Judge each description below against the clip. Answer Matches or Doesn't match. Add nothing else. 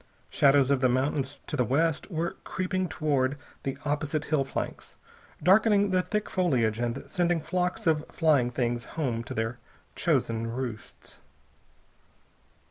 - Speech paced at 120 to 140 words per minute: Matches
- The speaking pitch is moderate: Matches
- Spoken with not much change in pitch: Doesn't match